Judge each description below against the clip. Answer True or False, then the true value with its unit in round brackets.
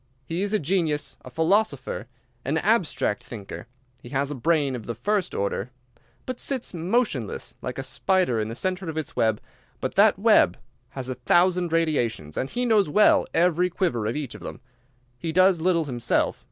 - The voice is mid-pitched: True (160 Hz)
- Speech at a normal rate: True (180 wpm)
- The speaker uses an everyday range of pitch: False (6.7 semitones)